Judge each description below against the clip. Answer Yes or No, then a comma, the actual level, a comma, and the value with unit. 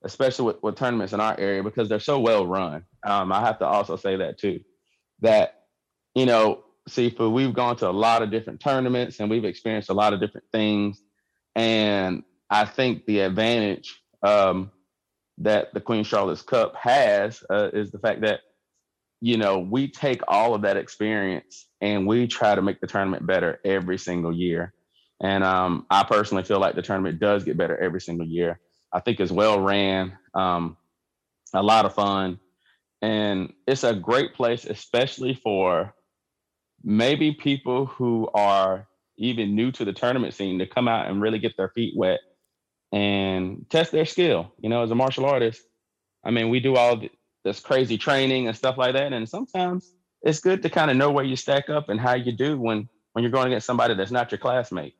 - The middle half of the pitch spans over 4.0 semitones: Yes, average, 4.4 semitones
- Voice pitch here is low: Yes, low, 110 Hz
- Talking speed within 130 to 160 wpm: No, average, 190 wpm